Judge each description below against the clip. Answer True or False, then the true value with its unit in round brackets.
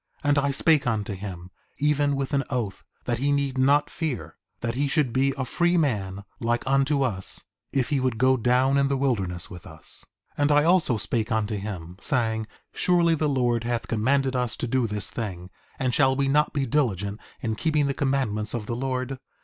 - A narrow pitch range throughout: False (4.3 semitones)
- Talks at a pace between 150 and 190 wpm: False (205 wpm)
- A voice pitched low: True (130 Hz)